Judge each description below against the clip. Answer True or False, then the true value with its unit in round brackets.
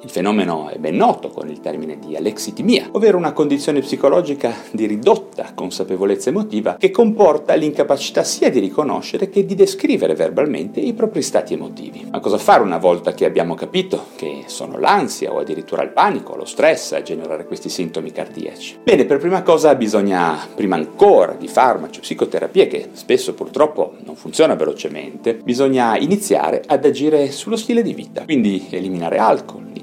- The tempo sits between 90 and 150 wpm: False (165 wpm)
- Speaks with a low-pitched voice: False (220 Hz)